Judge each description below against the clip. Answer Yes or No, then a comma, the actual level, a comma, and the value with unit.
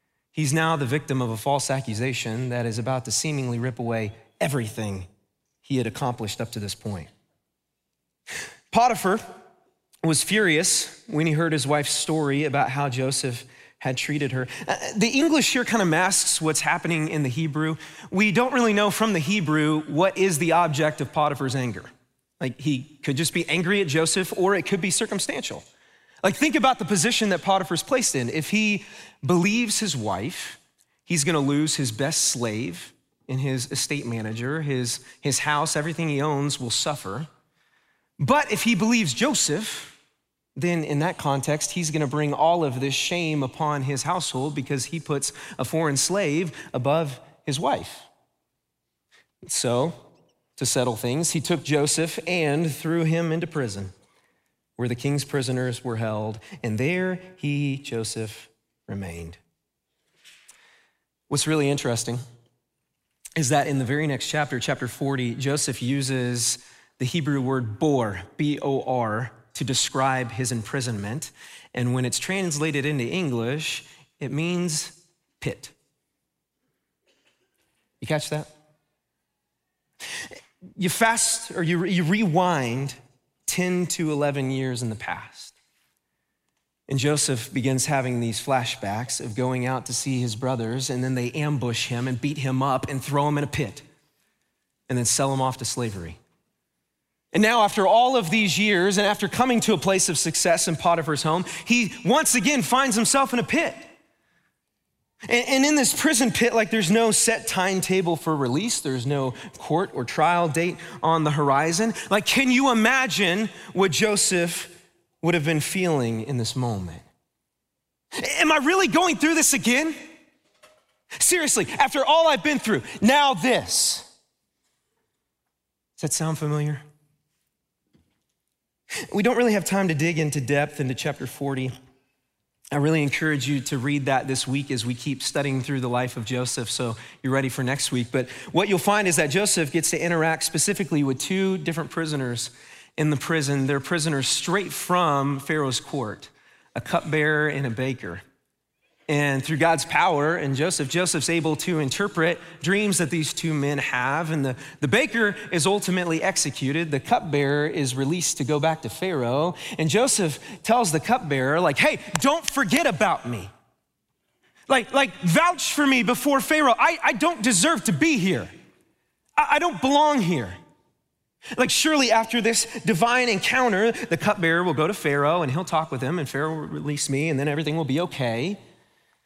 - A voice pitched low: No, medium, 155 Hz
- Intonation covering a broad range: Yes, wide, 5.9 semitones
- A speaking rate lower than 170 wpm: Yes, average, 160 wpm